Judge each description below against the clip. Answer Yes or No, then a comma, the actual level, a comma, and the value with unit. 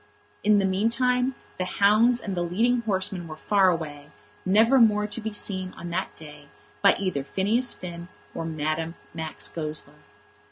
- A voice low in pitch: No, high, 190 Hz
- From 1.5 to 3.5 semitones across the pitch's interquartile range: No, average, 4.8 semitones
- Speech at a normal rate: Yes, average, 160 wpm